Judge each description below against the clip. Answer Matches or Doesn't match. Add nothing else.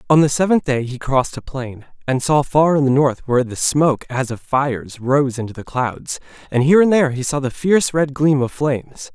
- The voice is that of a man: Matches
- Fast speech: Matches